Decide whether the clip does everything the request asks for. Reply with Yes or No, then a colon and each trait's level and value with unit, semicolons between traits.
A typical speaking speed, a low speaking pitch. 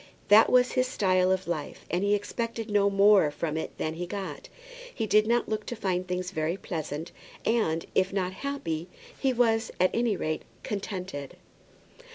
No: average, 175 wpm; high, 195 Hz